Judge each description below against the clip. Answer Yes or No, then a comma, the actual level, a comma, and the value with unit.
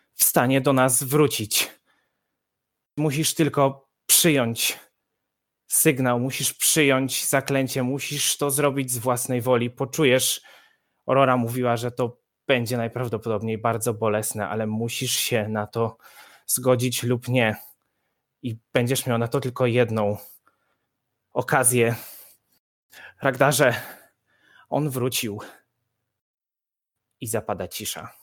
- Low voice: Yes, low, 125 Hz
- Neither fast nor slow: No, slow, 105 wpm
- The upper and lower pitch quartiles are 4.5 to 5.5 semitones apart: No, average, 2.7 semitones